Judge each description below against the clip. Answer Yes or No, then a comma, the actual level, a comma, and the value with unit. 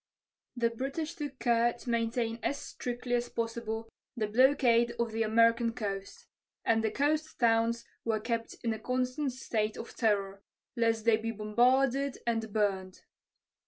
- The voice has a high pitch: Yes, high, 230 Hz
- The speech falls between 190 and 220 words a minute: No, average, 150 wpm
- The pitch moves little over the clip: Yes, narrow, 2.1 semitones